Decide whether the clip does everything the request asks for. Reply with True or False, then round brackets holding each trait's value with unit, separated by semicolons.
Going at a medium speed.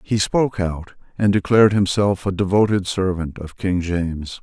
True (165 wpm)